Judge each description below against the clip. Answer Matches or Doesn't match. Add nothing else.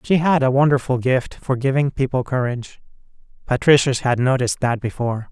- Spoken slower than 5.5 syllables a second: Doesn't match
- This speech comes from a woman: Doesn't match